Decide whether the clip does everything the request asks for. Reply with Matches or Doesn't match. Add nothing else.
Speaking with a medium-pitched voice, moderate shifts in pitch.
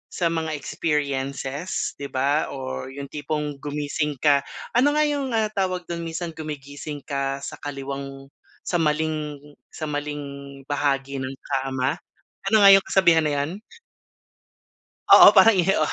Matches